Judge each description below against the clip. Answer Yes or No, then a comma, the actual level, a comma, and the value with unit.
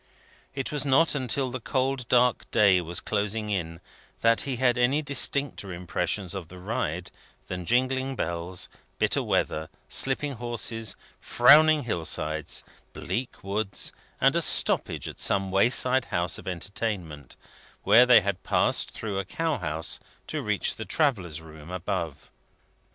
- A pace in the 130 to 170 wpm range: Yes, average, 145 wpm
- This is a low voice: Yes, low, 105 Hz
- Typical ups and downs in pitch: No, wide, 6.5 semitones